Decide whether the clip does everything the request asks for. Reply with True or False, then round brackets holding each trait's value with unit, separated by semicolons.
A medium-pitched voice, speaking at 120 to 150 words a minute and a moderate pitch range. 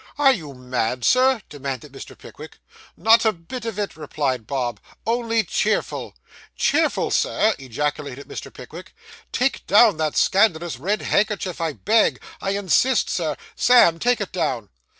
False (180 Hz; 145 wpm; 7.7 semitones)